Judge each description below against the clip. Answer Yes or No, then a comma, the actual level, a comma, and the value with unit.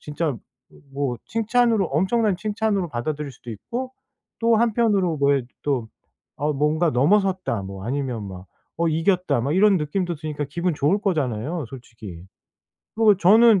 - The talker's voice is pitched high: No, medium, 160 Hz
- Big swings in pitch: Yes, wide, 6.9 semitones